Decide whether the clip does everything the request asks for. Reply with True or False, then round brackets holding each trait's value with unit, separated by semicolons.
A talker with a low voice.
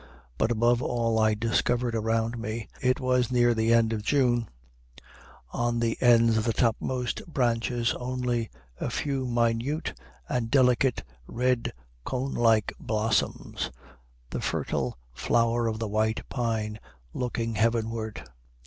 True (115 Hz)